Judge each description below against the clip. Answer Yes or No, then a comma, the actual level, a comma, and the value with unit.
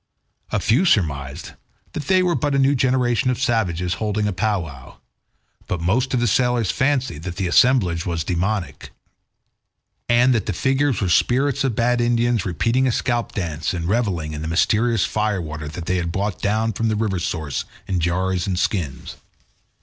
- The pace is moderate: Yes, average, 180 wpm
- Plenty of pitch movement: Yes, wide, 5.8 semitones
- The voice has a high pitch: No, low, 105 Hz